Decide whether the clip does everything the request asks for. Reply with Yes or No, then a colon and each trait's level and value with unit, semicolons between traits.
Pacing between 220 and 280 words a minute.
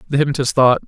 No: fast, 205 wpm